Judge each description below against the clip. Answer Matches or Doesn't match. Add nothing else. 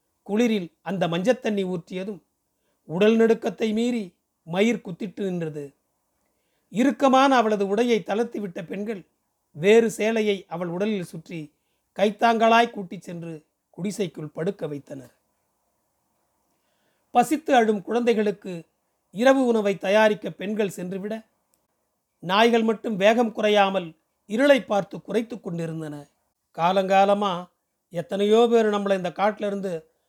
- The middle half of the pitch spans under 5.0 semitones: Matches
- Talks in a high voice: Matches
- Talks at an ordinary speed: Matches